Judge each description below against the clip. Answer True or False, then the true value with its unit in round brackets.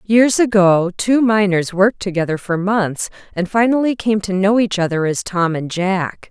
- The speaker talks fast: False (180 wpm)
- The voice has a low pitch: False (195 Hz)